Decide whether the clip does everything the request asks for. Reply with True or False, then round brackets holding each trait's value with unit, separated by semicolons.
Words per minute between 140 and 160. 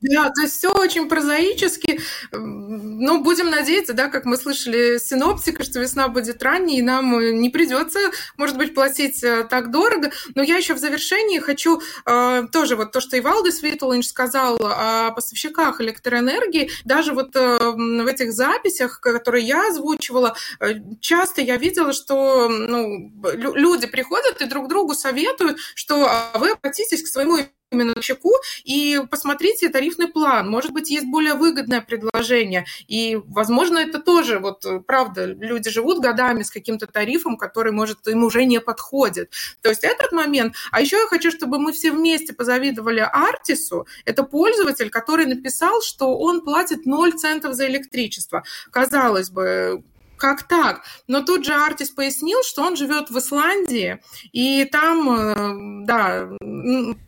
True (150 wpm)